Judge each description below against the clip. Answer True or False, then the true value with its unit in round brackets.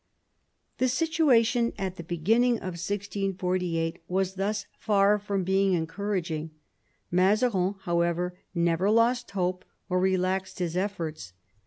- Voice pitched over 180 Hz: True (190 Hz)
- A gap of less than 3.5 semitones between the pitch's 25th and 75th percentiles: True (2.8 semitones)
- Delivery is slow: True (115 wpm)